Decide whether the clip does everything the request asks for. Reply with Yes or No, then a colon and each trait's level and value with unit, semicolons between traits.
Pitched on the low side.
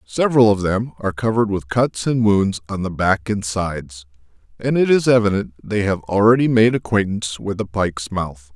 Yes: low, 100 Hz